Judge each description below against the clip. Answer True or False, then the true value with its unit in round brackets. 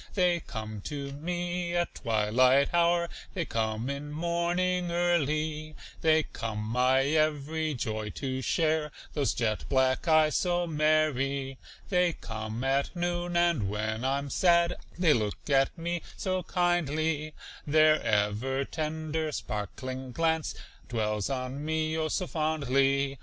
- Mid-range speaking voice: True (150 Hz)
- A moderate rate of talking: False (130 wpm)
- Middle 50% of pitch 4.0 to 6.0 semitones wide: True (4.6 semitones)